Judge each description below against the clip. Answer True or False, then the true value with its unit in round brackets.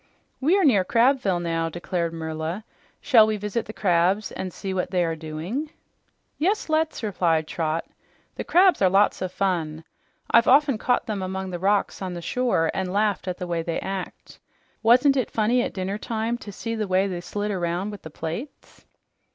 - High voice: True (195 Hz)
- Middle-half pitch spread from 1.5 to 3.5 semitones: False (4.7 semitones)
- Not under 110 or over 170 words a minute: False (185 wpm)